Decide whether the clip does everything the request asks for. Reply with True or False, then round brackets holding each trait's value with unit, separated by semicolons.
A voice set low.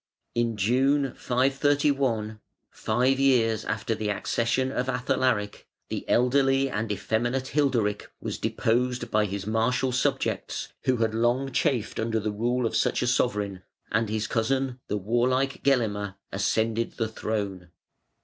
True (120 Hz)